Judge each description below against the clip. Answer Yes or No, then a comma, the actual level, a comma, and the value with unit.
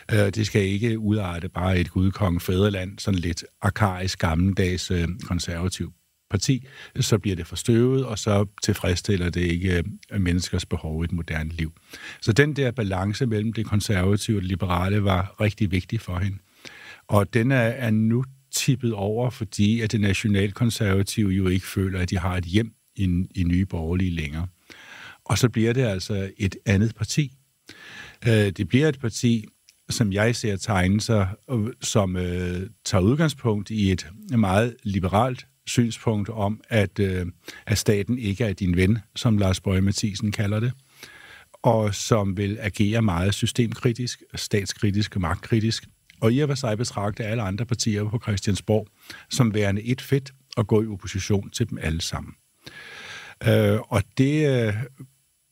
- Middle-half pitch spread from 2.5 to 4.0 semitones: Yes, average, 3.4 semitones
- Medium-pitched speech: No, low, 105 Hz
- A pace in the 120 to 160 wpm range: Yes, average, 155 wpm